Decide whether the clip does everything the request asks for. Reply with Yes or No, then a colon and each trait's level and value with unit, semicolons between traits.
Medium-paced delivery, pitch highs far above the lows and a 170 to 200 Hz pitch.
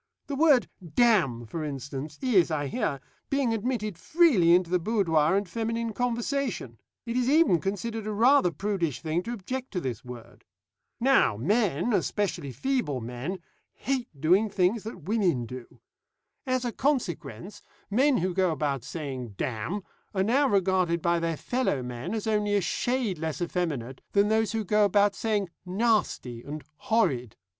Yes: average, 155 wpm; wide, 7.0 semitones; high, 190 Hz